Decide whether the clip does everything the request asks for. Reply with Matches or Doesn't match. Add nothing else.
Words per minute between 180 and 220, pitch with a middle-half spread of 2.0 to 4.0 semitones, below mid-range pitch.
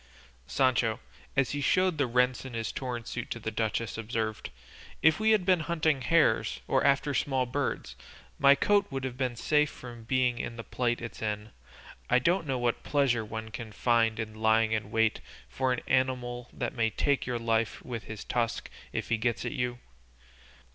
Matches